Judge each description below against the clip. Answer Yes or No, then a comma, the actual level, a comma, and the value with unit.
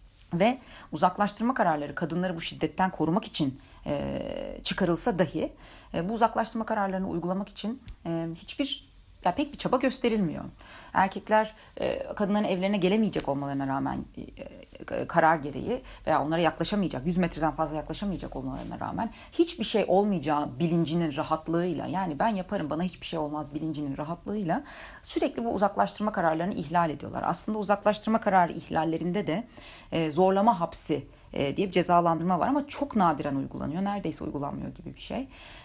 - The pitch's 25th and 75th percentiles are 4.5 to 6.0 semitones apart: Yes, average, 4.8 semitones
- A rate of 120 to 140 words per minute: Yes, average, 135 wpm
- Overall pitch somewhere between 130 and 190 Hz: Yes, medium, 185 Hz